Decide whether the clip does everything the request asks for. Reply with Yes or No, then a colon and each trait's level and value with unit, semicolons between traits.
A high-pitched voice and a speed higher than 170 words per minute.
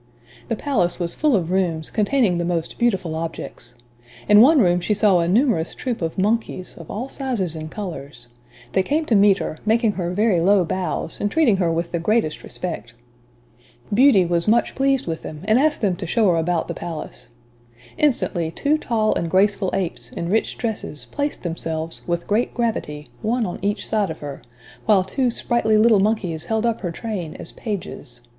Yes: high, 195 Hz; average, 190 wpm